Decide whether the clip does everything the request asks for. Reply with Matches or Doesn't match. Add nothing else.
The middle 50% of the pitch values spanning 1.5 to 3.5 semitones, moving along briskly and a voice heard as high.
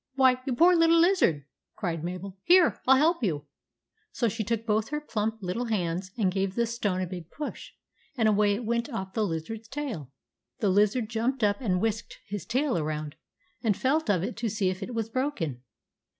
Doesn't match